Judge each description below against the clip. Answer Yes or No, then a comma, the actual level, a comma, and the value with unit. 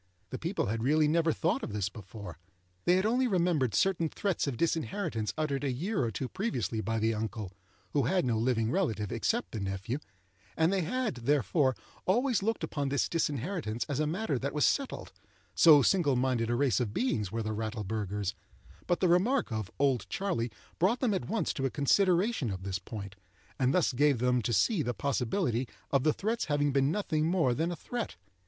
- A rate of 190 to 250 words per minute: Yes, average, 195 wpm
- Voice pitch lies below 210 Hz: Yes, medium, 140 Hz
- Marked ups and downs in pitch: Yes, wide, 7.7 semitones